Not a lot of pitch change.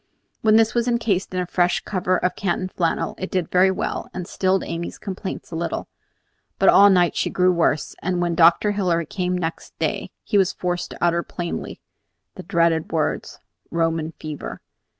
Yes: narrow, 2.1 semitones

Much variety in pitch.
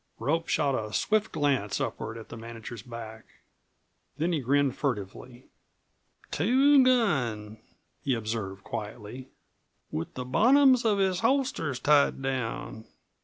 Yes: wide, 8.0 semitones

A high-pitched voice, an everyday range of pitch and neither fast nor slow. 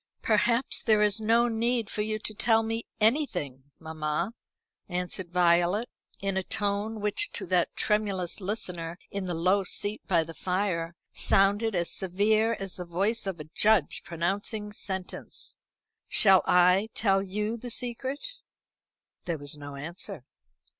Yes: high, 195 Hz; average, 3.8 semitones; average, 145 wpm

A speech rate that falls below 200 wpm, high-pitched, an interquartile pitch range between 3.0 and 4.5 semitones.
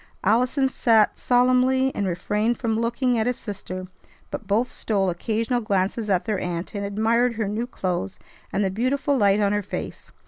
Yes: average, 175 wpm; high, 220 Hz; average, 3.6 semitones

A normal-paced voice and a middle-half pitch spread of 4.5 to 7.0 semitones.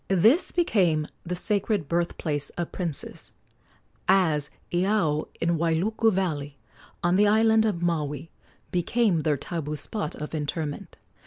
No: slow, 130 wpm; average, 4.9 semitones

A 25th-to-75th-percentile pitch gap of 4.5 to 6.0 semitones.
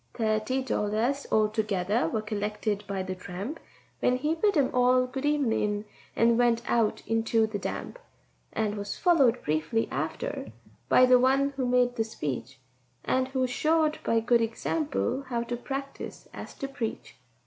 No: average, 3.9 semitones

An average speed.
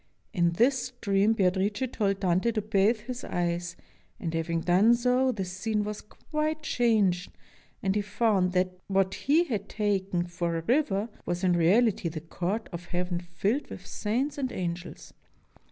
Yes: average, 160 wpm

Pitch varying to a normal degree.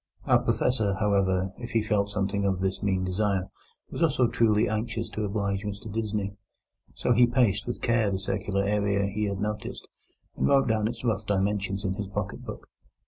No: narrow, 2.1 semitones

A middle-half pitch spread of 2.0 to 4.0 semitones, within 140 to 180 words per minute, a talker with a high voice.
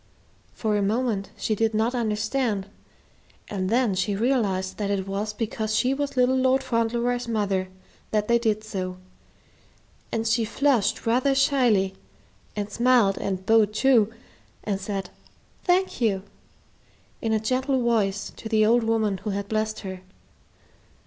Yes: average, 3.3 semitones; average, 145 wpm; high, 220 Hz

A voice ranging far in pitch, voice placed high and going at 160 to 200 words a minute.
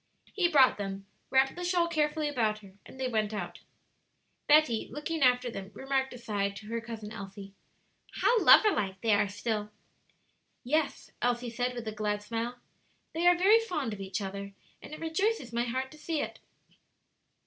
Yes: wide, 6.3 semitones; high, 245 Hz; average, 175 wpm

